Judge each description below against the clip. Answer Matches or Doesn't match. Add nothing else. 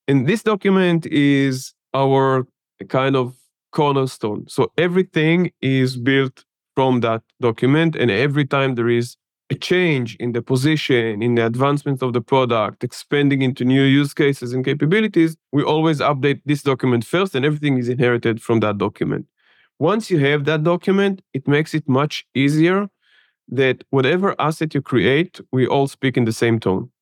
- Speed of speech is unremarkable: Matches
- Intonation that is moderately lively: Matches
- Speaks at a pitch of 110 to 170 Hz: Matches